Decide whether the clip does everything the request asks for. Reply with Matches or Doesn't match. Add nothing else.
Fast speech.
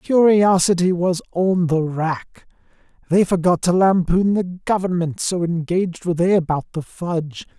Doesn't match